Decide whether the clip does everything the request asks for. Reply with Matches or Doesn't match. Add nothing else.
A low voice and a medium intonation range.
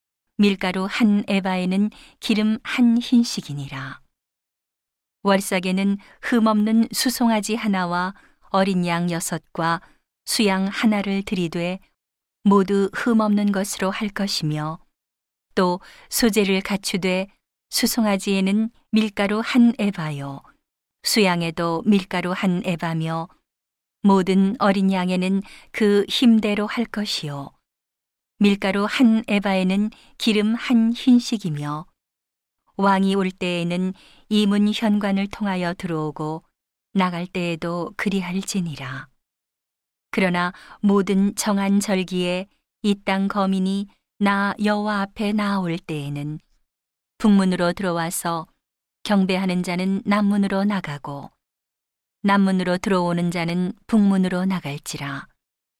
Doesn't match